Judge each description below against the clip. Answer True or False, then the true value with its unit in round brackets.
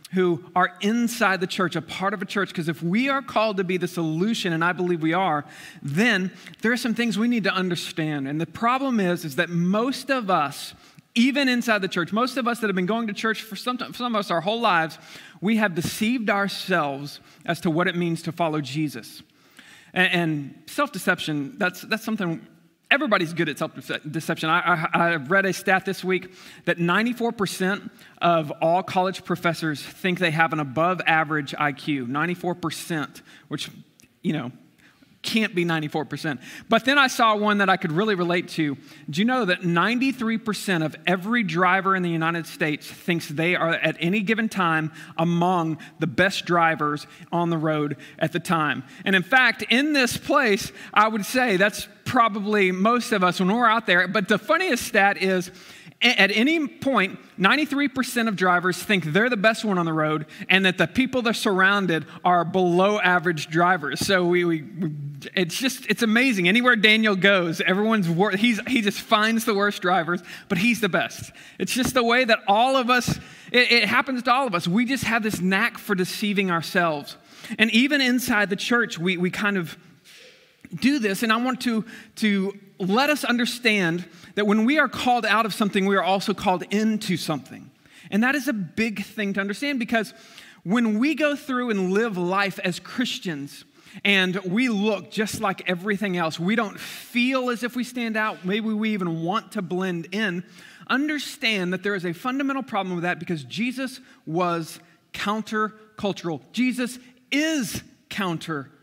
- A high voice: True (195 Hz)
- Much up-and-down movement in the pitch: False (4.7 semitones)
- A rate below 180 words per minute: False (185 wpm)